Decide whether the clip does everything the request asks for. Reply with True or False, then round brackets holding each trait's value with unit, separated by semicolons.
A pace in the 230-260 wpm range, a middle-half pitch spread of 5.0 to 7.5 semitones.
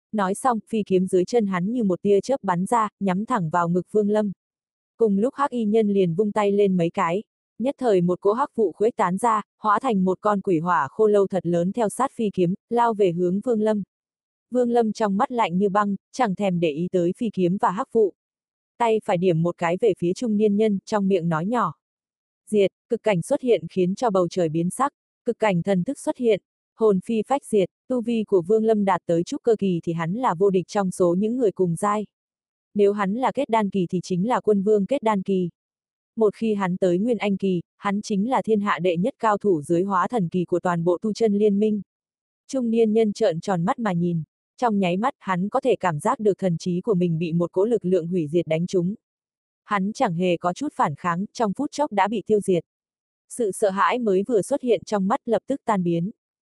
False (245 wpm; 3.6 semitones)